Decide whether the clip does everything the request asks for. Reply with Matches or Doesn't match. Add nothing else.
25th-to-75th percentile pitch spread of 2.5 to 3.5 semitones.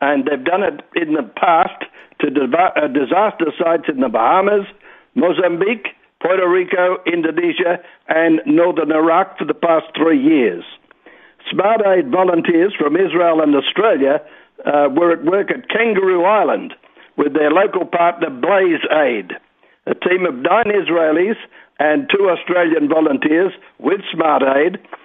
Matches